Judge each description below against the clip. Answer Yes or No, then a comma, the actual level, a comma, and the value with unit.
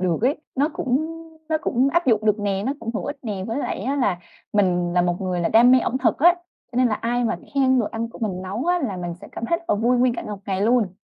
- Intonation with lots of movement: No, average, 5.0 semitones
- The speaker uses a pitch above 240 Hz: No, high, 230 Hz